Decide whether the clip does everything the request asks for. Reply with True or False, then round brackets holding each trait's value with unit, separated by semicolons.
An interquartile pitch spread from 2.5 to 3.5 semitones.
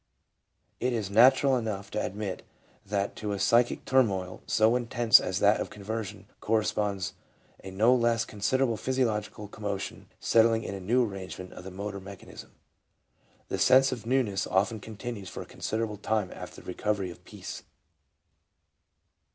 True (2.9 semitones)